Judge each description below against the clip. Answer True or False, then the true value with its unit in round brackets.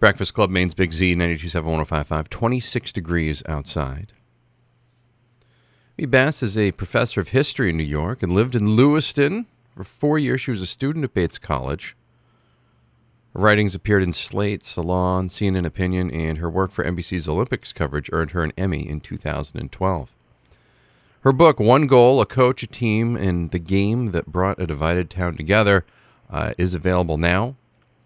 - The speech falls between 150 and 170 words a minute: True (160 wpm)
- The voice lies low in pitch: True (95 Hz)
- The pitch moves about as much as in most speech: False (5.8 semitones)